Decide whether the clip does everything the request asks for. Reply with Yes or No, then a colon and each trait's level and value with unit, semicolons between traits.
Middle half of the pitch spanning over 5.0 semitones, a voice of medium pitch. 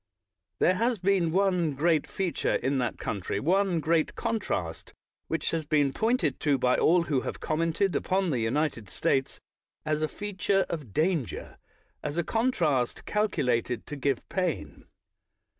Yes: wide, 5.5 semitones; medium, 160 Hz